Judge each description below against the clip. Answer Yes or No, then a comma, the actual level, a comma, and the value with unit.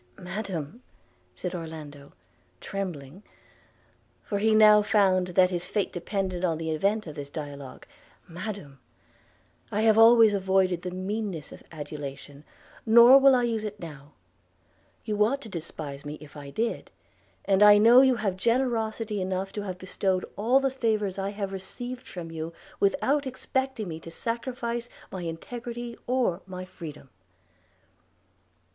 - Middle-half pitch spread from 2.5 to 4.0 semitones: No, average, 5.1 semitones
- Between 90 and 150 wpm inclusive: Yes, average, 145 wpm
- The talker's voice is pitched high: Yes, high, 195 Hz